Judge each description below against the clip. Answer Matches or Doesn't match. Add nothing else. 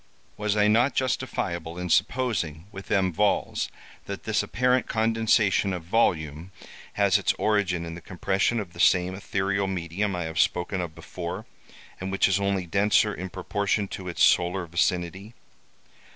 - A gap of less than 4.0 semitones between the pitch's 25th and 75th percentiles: Matches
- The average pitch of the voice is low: Matches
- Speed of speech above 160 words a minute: Doesn't match